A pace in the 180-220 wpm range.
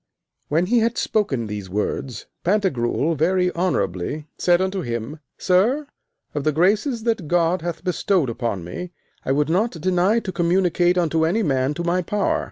No: average, 165 wpm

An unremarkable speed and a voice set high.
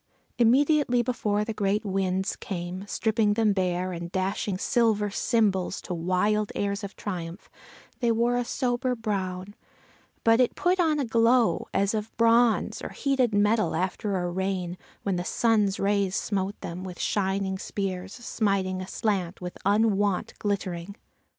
Yes: average, 145 wpm; high, 205 Hz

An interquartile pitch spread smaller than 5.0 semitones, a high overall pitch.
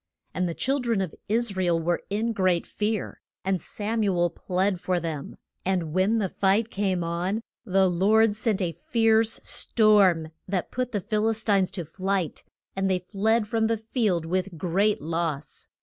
Yes: average, 3.6 semitones; high, 195 Hz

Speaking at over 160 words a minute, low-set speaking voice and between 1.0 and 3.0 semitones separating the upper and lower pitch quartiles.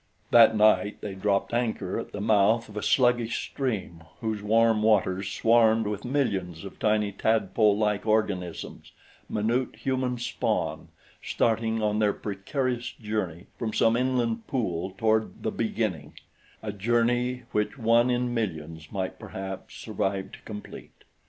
No: slow, 135 wpm; low, 110 Hz; average, 2.7 semitones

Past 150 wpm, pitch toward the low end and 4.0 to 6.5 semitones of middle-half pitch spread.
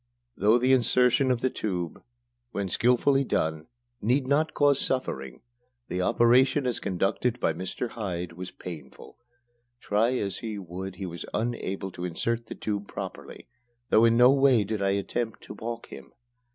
Yes: average, 160 wpm; low, 110 Hz; average, 4.8 semitones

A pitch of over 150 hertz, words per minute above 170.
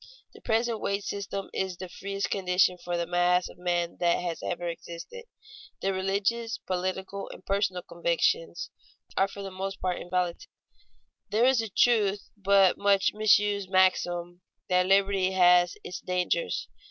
No: high, 190 Hz; average, 150 wpm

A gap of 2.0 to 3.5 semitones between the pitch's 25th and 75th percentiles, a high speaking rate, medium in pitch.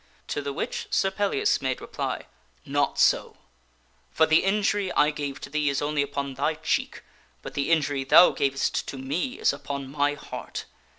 No: average, 3.0 semitones; average, 175 wpm; medium, 145 Hz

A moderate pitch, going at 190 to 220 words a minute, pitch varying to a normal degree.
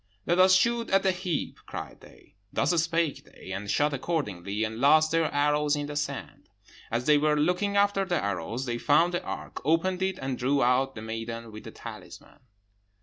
No: medium, 150 Hz; average, 195 wpm; wide, 6.5 semitones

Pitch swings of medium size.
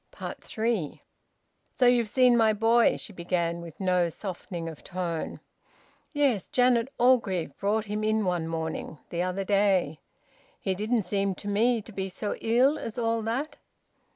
Yes: average, 4.3 semitones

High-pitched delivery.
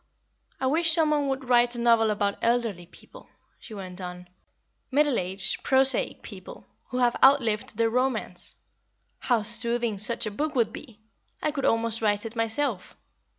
Yes: high, 235 Hz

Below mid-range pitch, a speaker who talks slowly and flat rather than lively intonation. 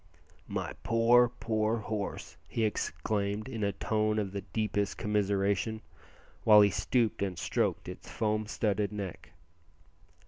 Yes: low, 105 Hz; slow, 130 wpm; narrow, 1.5 semitones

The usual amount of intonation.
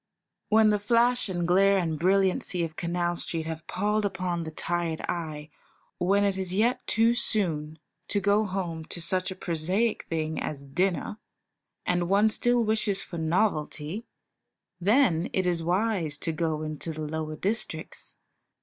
Yes: average, 4.0 semitones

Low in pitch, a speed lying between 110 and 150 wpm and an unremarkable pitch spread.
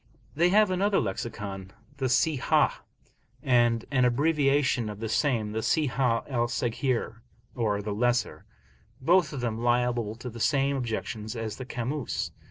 Yes: low, 120 Hz; average, 145 wpm; average, 3.6 semitones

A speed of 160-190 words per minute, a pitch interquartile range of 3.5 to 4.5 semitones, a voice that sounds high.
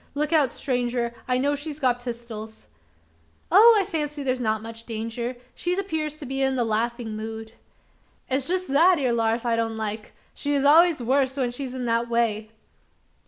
Yes: average, 175 wpm; average, 4.0 semitones; very high, 250 Hz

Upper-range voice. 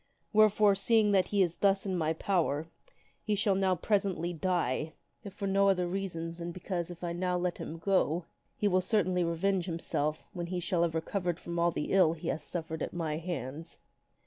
No: medium, 175 Hz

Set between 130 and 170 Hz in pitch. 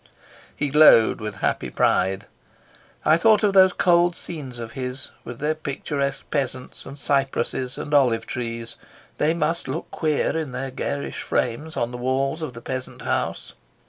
Yes: low, 135 Hz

